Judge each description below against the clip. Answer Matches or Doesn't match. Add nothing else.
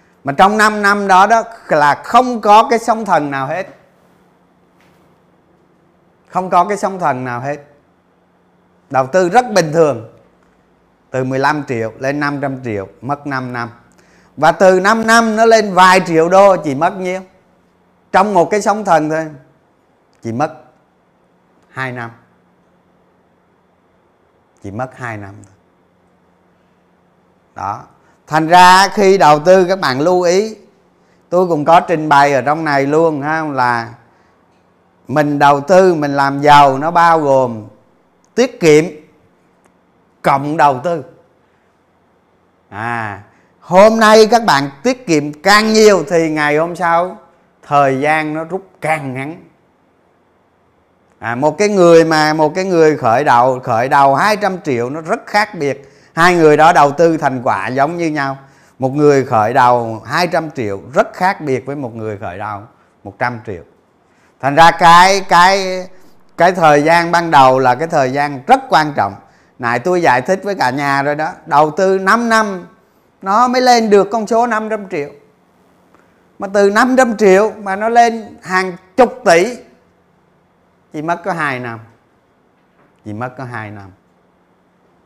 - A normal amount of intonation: Doesn't match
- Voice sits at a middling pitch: Matches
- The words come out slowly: Matches